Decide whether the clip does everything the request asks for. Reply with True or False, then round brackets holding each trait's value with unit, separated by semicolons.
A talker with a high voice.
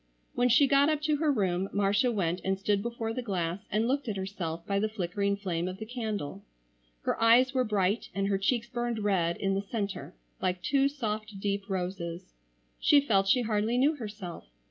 True (205 Hz)